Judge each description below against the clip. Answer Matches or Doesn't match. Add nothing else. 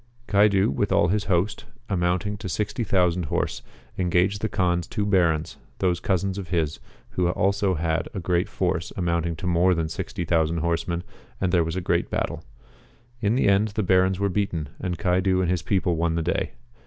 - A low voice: Matches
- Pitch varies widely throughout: Doesn't match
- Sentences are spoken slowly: Doesn't match